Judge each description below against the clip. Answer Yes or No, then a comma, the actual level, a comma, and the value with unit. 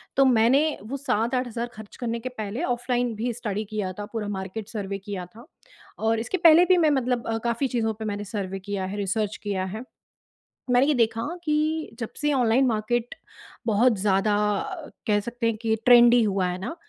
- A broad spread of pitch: No, average, 3.1 semitones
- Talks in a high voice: Yes, high, 225 Hz